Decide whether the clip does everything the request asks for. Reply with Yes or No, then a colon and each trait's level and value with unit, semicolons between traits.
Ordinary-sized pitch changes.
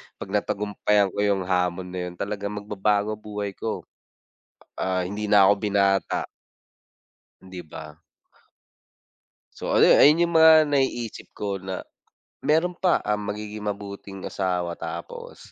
No: narrow, 2.1 semitones